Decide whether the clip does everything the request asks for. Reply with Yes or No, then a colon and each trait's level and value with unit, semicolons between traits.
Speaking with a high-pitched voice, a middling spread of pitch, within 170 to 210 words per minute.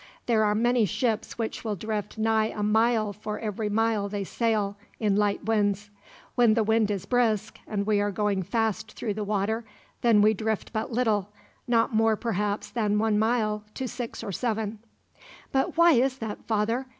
No: high, 215 Hz; narrow, 1.6 semitones; average, 180 wpm